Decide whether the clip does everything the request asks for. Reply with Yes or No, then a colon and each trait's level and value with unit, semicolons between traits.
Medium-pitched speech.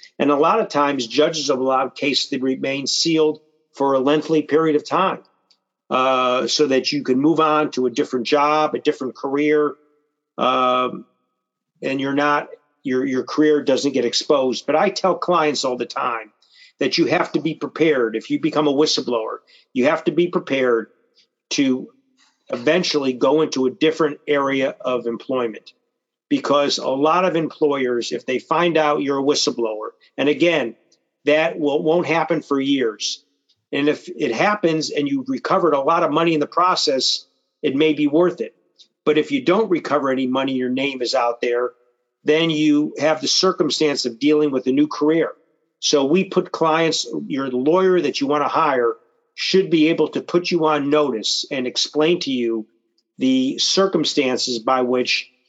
Yes: medium, 150 Hz